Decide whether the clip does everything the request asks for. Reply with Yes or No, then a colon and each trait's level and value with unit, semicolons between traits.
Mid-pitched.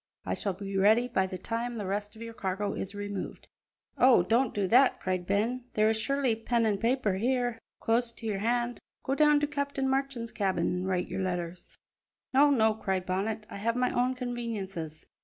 No: high, 225 Hz